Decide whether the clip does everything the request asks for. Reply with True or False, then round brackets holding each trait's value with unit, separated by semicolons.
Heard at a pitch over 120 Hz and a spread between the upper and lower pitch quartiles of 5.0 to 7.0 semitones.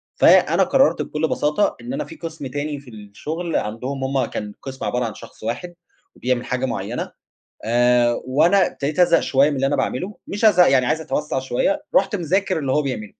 True (140 Hz; 5.3 semitones)